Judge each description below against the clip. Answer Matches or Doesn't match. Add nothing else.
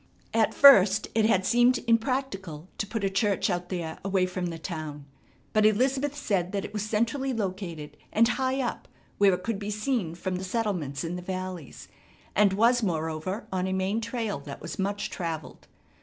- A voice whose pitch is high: Matches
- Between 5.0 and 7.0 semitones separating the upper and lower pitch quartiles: Doesn't match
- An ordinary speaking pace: Matches